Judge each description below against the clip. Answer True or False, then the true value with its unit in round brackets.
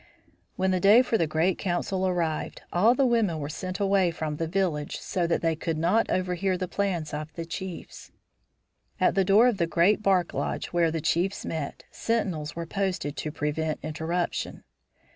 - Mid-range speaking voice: True (175 Hz)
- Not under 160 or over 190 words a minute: True (180 wpm)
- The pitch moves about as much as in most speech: True (3.3 semitones)